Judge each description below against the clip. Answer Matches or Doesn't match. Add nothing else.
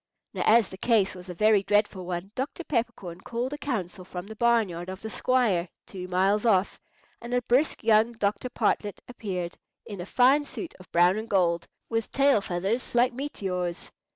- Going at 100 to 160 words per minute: Doesn't match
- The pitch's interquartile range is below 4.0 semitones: Doesn't match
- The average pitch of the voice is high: Matches